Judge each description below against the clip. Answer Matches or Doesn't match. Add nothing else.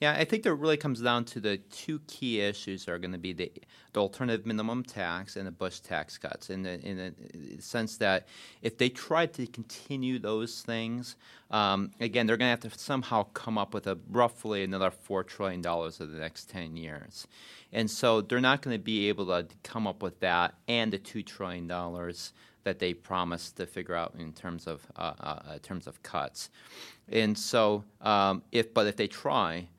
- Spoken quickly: Matches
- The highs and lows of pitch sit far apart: Doesn't match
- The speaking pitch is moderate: Doesn't match